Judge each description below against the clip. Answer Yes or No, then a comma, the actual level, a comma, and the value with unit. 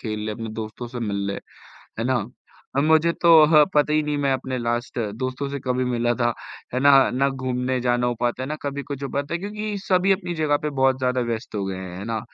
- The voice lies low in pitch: Yes, low, 130 Hz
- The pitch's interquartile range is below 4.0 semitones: Yes, average, 3.5 semitones